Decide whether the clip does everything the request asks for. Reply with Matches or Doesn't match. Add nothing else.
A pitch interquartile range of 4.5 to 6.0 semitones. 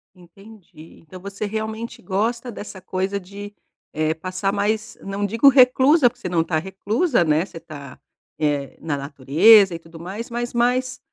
Matches